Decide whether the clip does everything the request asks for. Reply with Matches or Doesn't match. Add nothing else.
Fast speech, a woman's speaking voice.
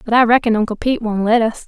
Matches